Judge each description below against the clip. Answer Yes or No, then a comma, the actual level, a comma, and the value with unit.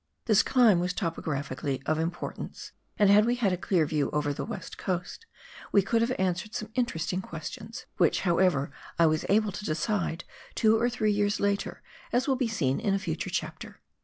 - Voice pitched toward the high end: Yes, high, 195 Hz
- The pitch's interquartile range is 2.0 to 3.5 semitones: No, average, 4.9 semitones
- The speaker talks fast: No, average, 190 wpm